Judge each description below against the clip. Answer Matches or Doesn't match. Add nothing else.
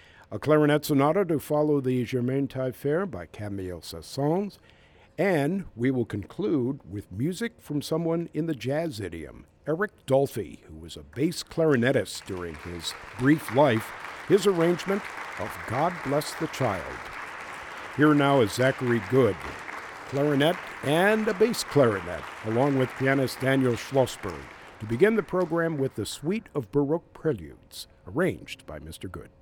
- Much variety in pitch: Matches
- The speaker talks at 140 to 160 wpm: Matches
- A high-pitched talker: Doesn't match